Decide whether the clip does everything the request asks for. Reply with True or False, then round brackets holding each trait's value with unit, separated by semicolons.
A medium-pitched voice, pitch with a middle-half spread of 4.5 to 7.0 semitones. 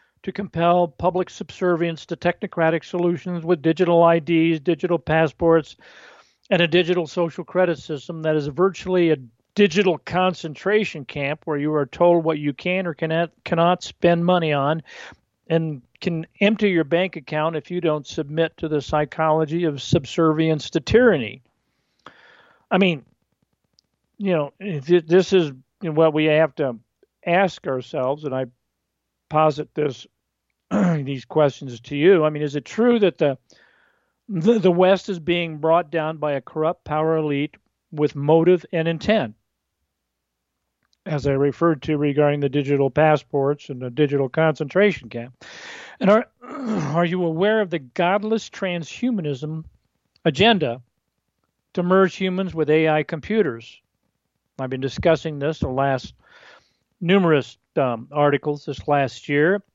False (160 Hz; 3.6 semitones)